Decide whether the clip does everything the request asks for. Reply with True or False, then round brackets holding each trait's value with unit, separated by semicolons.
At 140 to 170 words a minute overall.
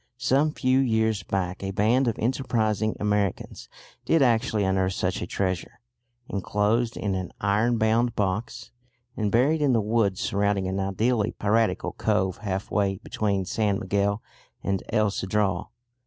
True (145 wpm)